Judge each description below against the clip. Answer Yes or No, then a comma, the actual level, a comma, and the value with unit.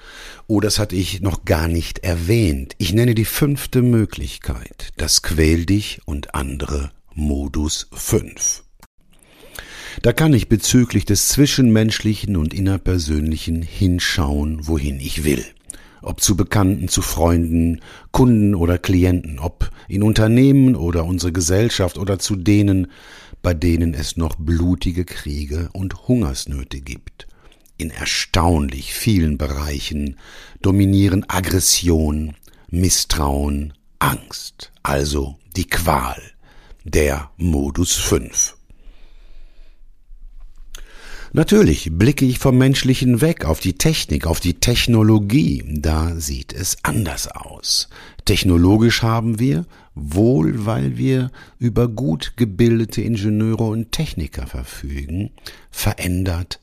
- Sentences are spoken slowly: Yes, slow, 110 wpm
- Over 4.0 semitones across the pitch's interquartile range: Yes, wide, 5.6 semitones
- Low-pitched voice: Yes, very low, 90 Hz